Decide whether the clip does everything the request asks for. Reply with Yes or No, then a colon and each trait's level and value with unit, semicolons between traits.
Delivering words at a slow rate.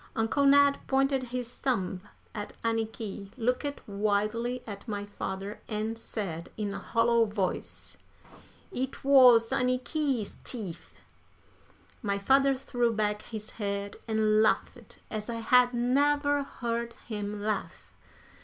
Yes: slow, 120 wpm